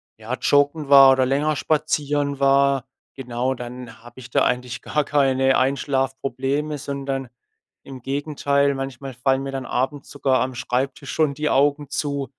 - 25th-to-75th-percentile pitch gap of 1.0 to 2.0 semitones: Yes, narrow, 1.5 semitones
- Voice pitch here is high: No, low, 135 Hz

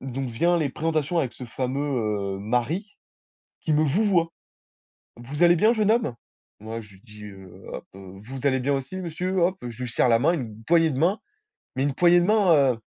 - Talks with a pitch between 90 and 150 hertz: Yes, medium, 140 Hz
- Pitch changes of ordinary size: No, wide, 6.6 semitones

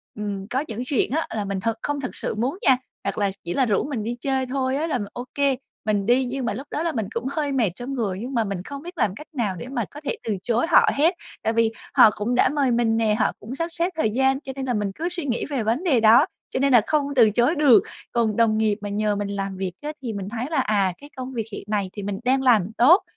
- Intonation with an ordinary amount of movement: Yes, average, 4.4 semitones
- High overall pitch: Yes, high, 240 Hz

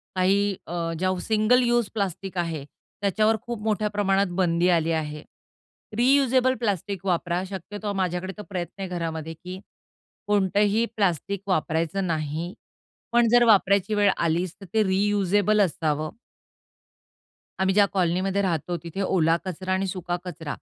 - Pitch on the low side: No, high, 190 Hz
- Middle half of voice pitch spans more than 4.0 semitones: No, average, 3.1 semitones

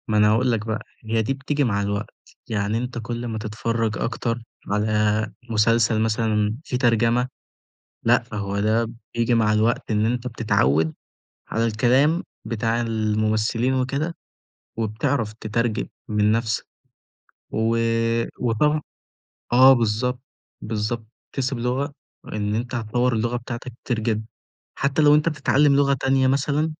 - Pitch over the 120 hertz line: No, low, 115 Hz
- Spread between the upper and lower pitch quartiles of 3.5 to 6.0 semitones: No, average, 2.7 semitones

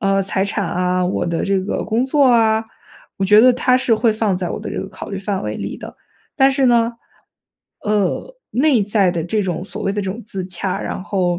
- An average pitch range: Yes, average, 3.6 semitones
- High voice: Yes, high, 205 Hz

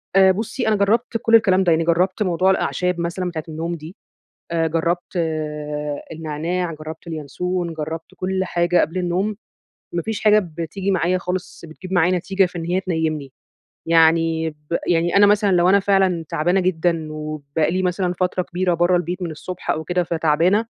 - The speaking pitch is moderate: Yes, medium, 175 Hz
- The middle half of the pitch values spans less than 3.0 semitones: Yes, narrow, 2.4 semitones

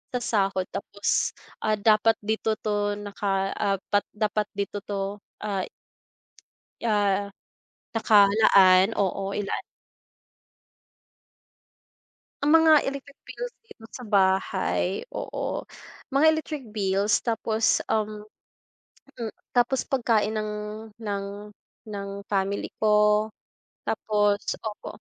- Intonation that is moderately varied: No, narrow, 1.9 semitones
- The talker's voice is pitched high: Yes, high, 210 Hz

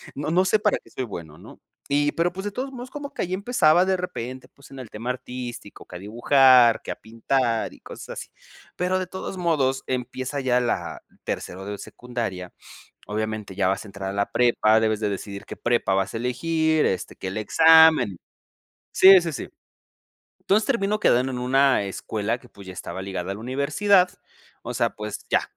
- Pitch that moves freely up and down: Yes, wide, 7.6 semitones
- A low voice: Yes, low, 125 Hz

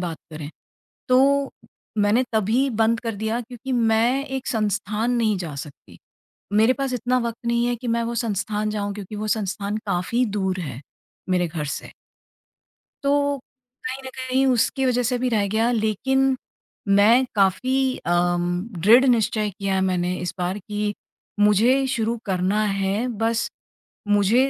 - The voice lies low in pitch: No, high, 220 Hz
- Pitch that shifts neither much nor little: Yes, average, 3.7 semitones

